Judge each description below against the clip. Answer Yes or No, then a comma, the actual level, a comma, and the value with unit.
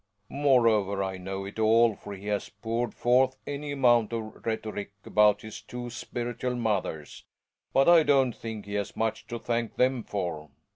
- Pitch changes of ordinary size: Yes, average, 3.1 semitones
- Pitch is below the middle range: Yes, low, 115 Hz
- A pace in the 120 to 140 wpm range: No, average, 165 wpm